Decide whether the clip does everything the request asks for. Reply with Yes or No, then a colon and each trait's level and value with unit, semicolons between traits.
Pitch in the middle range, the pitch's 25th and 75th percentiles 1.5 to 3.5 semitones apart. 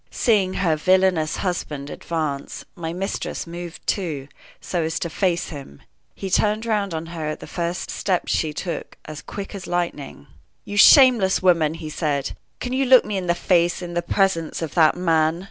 Yes: medium, 175 Hz; average, 3.2 semitones